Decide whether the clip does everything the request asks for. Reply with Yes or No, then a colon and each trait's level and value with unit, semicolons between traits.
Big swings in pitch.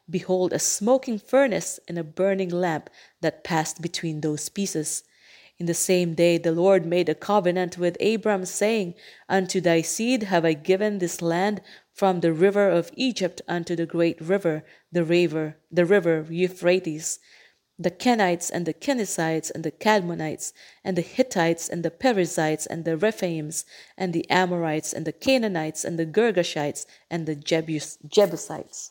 No: average, 2.9 semitones